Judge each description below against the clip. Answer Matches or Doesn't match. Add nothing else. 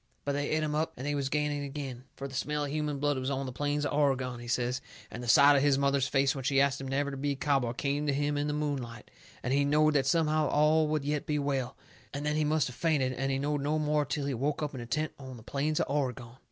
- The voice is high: Doesn't match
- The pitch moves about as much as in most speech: Doesn't match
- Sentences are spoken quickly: Matches